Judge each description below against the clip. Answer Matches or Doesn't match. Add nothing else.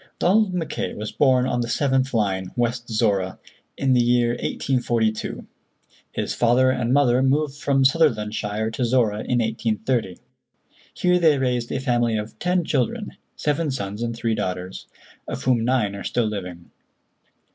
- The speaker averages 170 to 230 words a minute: Doesn't match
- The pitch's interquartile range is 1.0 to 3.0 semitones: Doesn't match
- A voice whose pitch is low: Matches